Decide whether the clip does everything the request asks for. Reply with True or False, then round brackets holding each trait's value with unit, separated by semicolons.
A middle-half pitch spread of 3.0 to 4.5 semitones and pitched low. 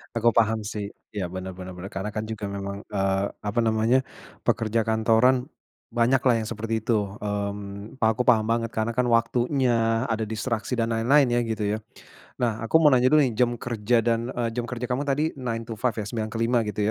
False (2.4 semitones; 115 Hz)